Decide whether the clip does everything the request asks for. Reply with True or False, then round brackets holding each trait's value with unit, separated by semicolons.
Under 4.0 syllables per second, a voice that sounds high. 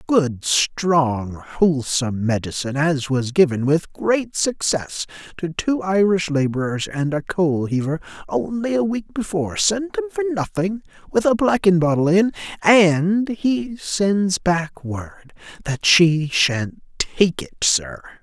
False (3.8 syllables/s; 165 Hz)